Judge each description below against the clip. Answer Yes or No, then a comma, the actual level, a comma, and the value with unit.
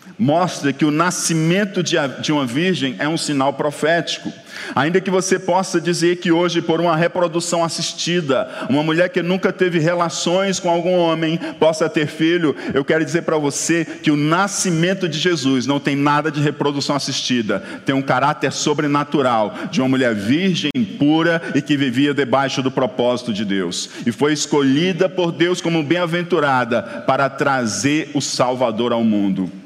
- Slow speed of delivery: No, average, 160 wpm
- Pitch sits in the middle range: Yes, medium, 160 Hz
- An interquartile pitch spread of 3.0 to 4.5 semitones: Yes, average, 3.7 semitones